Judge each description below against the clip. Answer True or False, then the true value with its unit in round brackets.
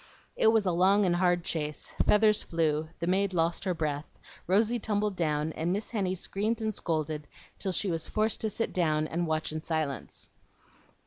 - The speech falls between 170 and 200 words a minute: True (185 wpm)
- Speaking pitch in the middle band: True (175 Hz)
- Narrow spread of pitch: False (4.6 semitones)